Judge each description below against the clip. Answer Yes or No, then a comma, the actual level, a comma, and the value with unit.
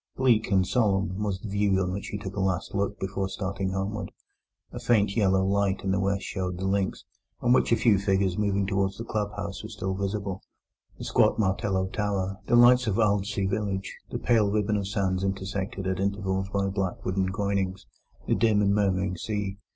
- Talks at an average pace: Yes, average, 195 wpm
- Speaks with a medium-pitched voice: No, low, 100 Hz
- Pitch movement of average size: No, narrow, 1.4 semitones